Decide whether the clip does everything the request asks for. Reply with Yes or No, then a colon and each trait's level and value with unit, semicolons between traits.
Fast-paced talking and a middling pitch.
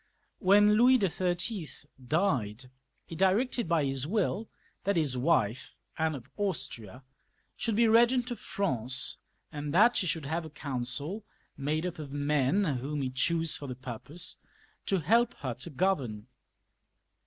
No: average, 145 wpm; medium, 160 Hz